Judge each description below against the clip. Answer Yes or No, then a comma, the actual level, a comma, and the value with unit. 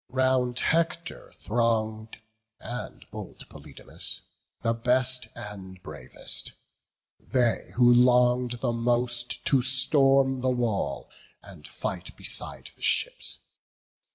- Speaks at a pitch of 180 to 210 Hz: No, low, 125 Hz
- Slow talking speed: Yes, slow, 100 wpm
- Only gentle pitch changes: Yes, narrow, 2.0 semitones